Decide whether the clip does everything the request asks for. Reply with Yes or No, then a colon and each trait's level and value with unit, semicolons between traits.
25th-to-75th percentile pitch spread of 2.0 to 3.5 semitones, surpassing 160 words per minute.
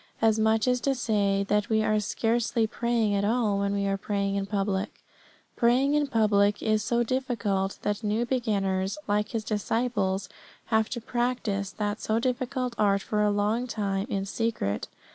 Yes: average, 2.8 semitones; average, 170 wpm